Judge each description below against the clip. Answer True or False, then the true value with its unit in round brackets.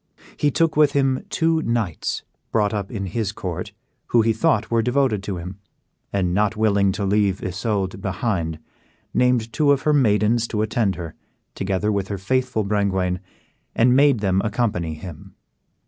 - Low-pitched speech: True (105 Hz)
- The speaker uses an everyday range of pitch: True (4.1 semitones)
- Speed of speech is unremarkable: True (160 wpm)